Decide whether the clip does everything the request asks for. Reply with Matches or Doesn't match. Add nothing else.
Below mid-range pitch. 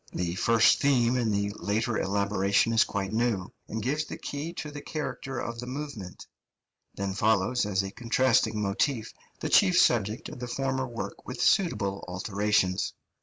Matches